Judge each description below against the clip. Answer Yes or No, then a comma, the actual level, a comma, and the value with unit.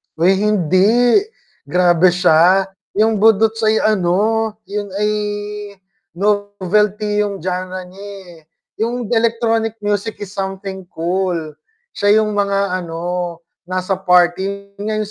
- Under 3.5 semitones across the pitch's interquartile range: Yes, average, 2.7 semitones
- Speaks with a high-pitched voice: Yes, high, 200 Hz